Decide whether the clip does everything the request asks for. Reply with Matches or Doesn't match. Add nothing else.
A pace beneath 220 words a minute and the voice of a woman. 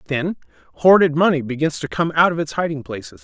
Doesn't match